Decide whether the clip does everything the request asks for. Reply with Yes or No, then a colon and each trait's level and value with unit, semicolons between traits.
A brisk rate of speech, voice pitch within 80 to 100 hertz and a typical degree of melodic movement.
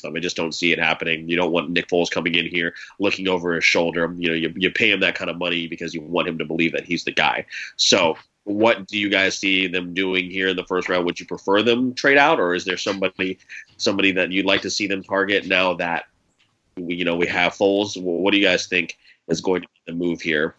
No: fast, 260 wpm; very low, 90 Hz; narrow, 2.2 semitones